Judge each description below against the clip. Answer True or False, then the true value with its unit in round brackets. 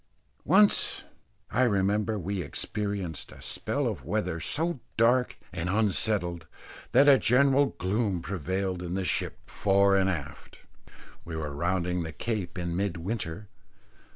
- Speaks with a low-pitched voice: True (95 Hz)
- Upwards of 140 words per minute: False (135 wpm)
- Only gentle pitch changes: False (3.9 semitones)